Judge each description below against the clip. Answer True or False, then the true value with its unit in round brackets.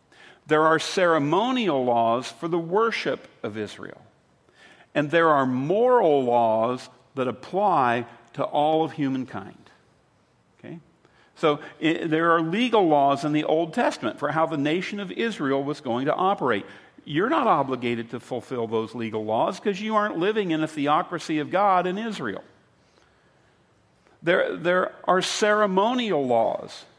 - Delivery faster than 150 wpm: False (145 wpm)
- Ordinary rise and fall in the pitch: False (6.0 semitones)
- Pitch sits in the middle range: True (155 Hz)